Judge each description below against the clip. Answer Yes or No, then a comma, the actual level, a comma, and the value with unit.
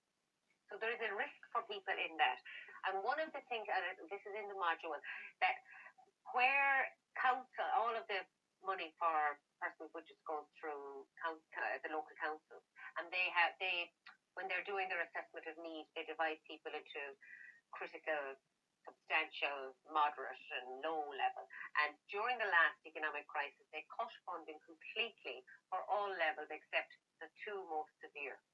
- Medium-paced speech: Yes, average, 160 wpm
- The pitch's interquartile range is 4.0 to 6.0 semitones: Yes, average, 5.3 semitones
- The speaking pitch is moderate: Yes, medium, 165 Hz